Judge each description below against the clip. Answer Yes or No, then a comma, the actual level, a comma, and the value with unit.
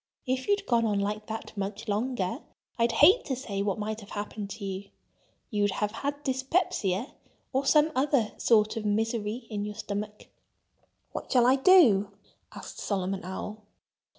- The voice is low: No, high, 215 Hz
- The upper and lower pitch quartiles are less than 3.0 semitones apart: No, average, 4.1 semitones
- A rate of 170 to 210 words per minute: No, average, 160 wpm